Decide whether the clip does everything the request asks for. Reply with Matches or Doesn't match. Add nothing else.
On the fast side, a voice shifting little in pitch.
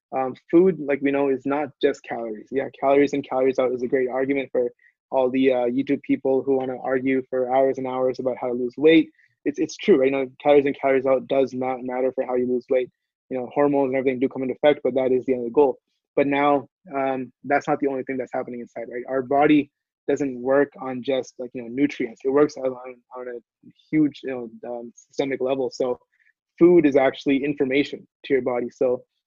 Matches